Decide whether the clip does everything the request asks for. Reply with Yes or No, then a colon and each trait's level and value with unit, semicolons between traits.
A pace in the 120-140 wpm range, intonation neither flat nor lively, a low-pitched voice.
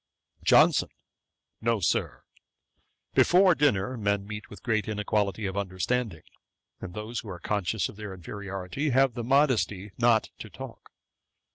Yes: slow, 135 wpm; average, 3.6 semitones; low, 105 Hz